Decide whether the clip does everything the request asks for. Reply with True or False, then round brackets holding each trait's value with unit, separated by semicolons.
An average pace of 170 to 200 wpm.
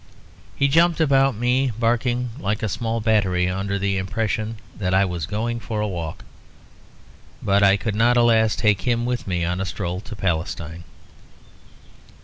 False (160 wpm)